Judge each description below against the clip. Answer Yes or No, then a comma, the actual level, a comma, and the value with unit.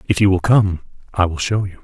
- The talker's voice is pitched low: Yes, very low, 95 Hz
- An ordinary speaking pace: No, fast, 260 wpm